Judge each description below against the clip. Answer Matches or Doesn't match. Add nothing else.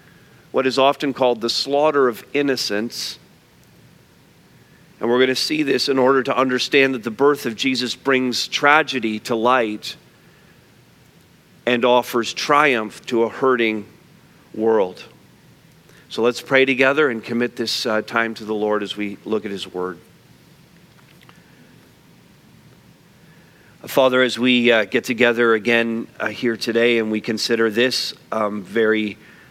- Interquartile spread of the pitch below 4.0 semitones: Matches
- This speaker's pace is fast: Doesn't match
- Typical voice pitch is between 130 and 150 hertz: Doesn't match